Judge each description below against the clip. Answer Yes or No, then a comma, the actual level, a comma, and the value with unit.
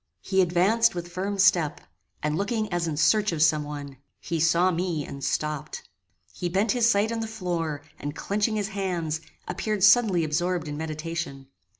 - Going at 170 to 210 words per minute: Yes, average, 175 wpm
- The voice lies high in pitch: No, medium, 175 Hz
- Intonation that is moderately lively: Yes, average, 4.5 semitones